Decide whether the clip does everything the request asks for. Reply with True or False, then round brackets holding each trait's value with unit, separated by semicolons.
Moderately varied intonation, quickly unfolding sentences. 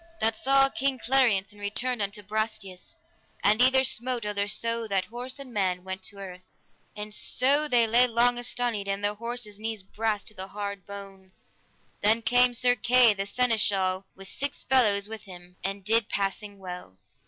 False (3.6 semitones; 175 wpm)